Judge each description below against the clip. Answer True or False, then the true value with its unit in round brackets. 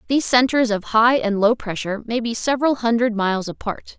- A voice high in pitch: True (230 Hz)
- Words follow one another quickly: False (195 wpm)